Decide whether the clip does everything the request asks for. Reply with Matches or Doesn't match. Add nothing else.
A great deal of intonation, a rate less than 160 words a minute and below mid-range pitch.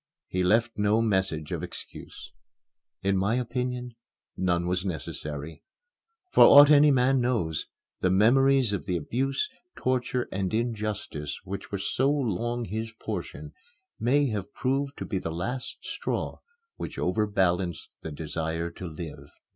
Matches